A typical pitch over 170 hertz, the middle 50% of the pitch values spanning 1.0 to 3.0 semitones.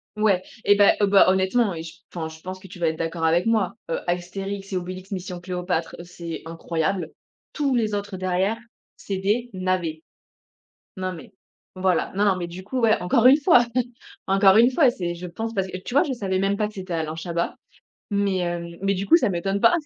Yes: high, 190 Hz; average, 2.7 semitones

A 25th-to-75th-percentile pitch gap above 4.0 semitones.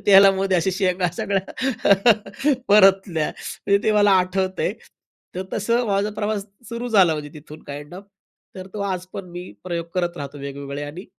No: average, 2.8 semitones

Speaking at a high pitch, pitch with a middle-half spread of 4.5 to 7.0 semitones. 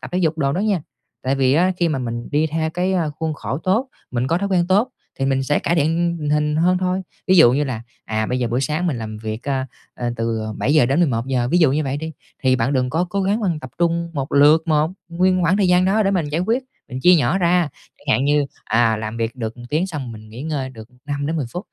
No: medium, 150 Hz; average, 5.3 semitones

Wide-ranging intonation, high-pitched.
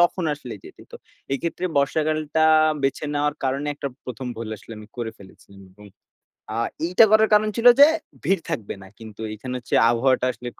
No: wide, 5.8 semitones; low, 135 Hz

